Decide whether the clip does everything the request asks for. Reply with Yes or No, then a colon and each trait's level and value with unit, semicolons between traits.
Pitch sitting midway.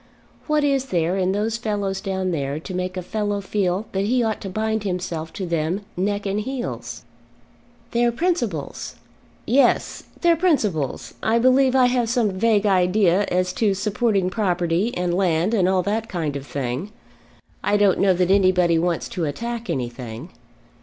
No: high, 195 Hz